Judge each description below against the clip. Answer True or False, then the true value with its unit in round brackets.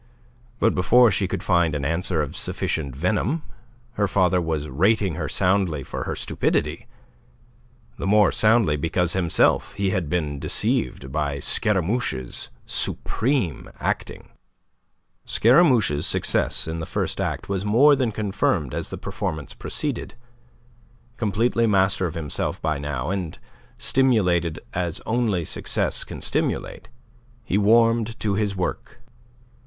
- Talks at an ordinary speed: False (130 wpm)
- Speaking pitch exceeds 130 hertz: False (95 Hz)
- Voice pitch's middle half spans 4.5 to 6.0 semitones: True (5.2 semitones)